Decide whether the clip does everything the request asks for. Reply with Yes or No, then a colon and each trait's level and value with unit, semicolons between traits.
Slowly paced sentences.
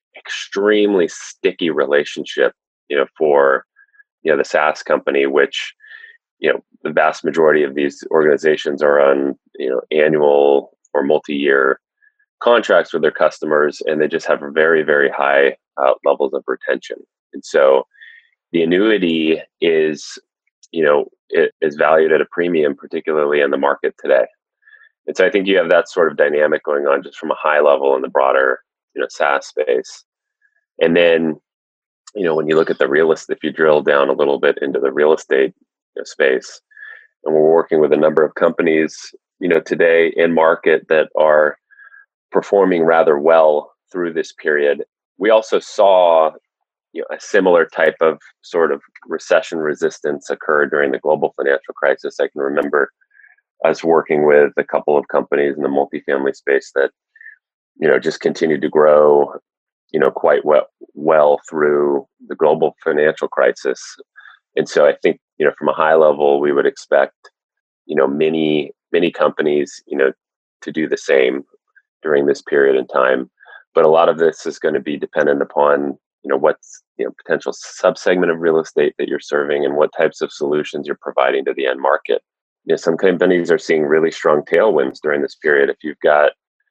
No: average, 180 wpm